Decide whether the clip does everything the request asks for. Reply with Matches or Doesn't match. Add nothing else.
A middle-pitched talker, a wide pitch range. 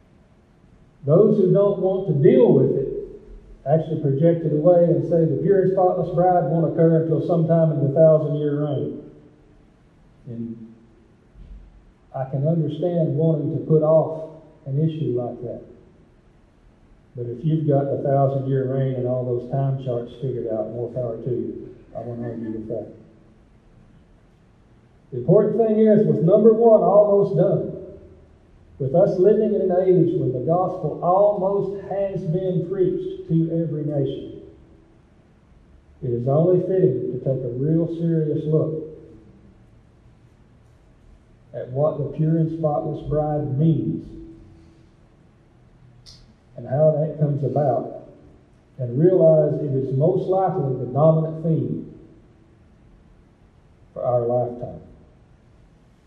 Matches